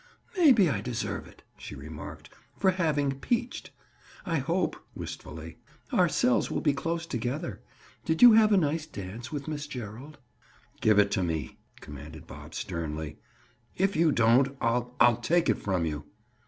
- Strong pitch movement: Yes, wide, 8.9 semitones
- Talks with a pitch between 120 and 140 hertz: Yes, low, 135 Hz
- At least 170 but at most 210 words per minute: No, average, 155 wpm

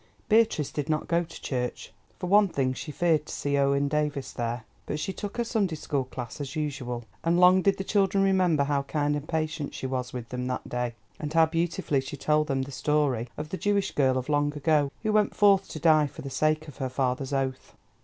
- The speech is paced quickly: Yes, fast, 225 wpm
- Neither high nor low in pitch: Yes, medium, 150 Hz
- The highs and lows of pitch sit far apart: No, average, 4.0 semitones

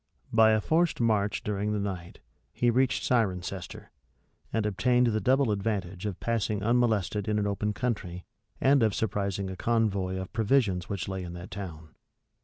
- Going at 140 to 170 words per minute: Yes, average, 160 wpm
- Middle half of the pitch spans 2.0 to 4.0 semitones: Yes, average, 3.3 semitones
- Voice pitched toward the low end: Yes, low, 105 Hz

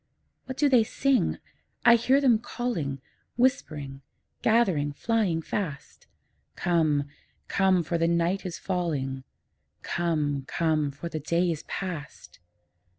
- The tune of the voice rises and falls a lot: Yes, wide, 6.8 semitones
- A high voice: No, medium, 170 Hz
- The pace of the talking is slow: Yes, slow, 120 wpm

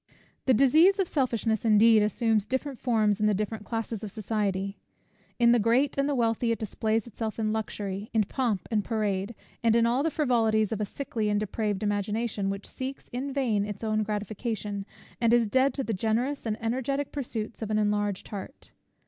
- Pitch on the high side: Yes, high, 220 Hz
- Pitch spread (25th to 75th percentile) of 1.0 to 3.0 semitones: Yes, narrow, 2.6 semitones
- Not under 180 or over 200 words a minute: Yes, average, 190 wpm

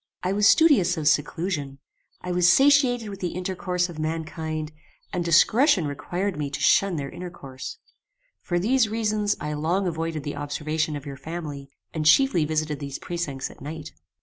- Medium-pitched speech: Yes, medium, 165 Hz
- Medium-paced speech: Yes, average, 165 wpm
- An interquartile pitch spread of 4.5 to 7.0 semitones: No, average, 4.0 semitones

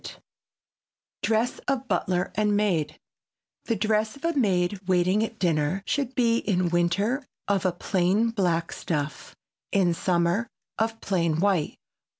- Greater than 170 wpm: No, average, 140 wpm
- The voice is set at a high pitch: Yes, high, 195 Hz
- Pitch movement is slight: No, average, 4.2 semitones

